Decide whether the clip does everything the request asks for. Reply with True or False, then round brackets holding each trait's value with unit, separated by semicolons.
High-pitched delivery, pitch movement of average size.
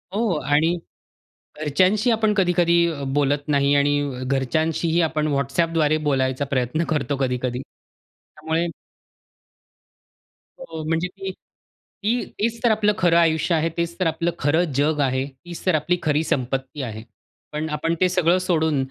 False (160 Hz; 3.4 semitones)